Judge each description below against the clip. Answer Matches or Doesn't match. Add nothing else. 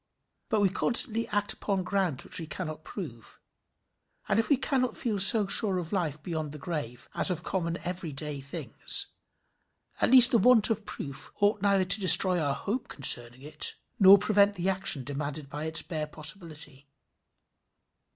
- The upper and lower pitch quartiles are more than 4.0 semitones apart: Matches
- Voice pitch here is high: Doesn't match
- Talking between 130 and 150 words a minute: Doesn't match